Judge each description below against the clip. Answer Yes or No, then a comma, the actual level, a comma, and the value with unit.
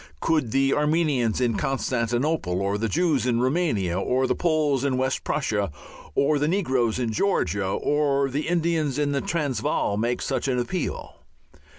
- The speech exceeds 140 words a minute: Yes, average, 160 wpm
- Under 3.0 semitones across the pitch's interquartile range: No, average, 4.4 semitones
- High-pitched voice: No, low, 135 Hz